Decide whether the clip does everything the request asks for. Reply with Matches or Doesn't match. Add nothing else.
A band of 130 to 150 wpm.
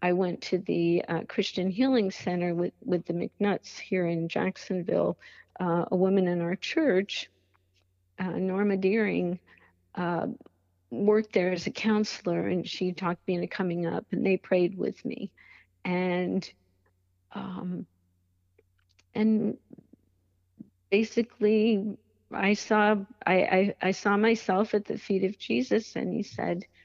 Matches